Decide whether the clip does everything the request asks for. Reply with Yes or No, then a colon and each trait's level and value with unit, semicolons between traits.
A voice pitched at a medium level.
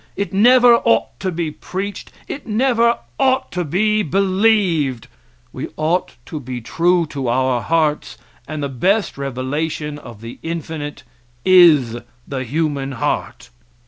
Yes: medium, 160 Hz